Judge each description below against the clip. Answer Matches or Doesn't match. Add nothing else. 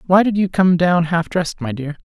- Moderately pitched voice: Matches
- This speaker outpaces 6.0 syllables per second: Doesn't match